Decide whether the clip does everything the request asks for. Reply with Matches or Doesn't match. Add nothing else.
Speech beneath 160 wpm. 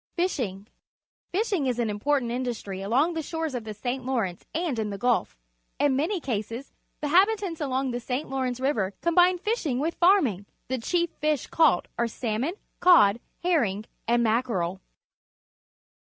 Doesn't match